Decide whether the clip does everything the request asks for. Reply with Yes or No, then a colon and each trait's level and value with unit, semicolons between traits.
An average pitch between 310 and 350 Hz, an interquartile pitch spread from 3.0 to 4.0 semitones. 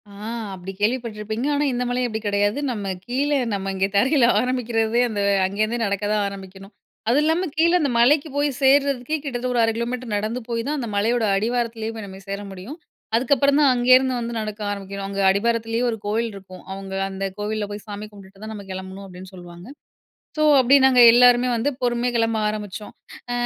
No: high, 225 Hz; average, 3.7 semitones